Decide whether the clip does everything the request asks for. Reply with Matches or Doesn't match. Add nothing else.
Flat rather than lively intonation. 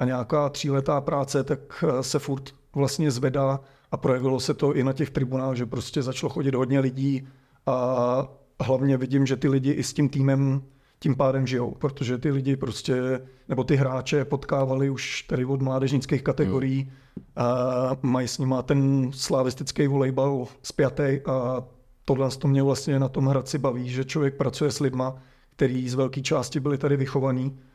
Matches